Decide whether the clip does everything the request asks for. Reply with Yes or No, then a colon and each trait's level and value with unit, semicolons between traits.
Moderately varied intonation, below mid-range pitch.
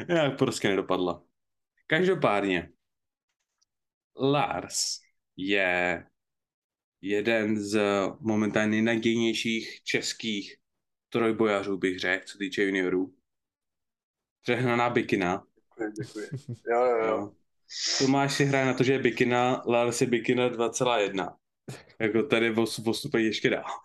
Yes: average, 3.3 semitones; low, 110 Hz